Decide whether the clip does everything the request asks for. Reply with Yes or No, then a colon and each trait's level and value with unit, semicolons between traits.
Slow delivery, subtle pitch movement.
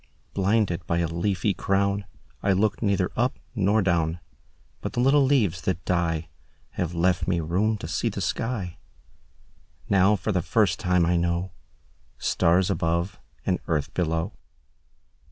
No: slow, 125 wpm; average, 3.2 semitones